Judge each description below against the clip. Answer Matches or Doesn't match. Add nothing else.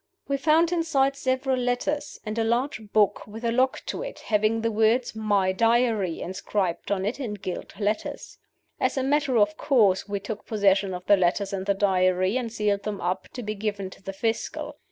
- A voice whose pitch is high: Matches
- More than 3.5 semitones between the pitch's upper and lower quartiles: Matches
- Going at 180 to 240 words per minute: Matches